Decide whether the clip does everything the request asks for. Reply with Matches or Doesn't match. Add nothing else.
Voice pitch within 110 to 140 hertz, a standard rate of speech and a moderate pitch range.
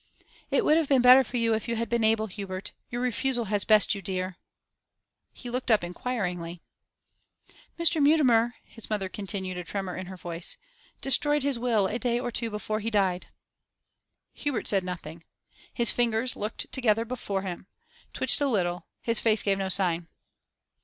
Doesn't match